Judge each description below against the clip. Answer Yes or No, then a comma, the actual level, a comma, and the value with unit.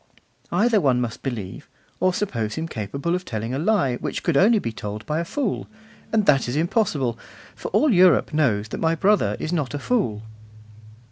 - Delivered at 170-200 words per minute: Yes, average, 190 wpm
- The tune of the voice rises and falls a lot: Yes, wide, 7.8 semitones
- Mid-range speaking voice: Yes, medium, 150 Hz